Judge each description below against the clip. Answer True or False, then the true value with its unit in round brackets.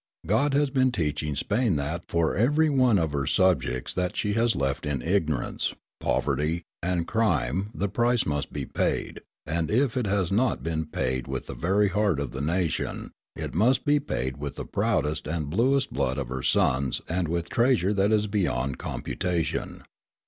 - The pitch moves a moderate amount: False (6.8 semitones)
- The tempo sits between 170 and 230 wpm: True (180 wpm)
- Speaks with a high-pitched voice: False (90 Hz)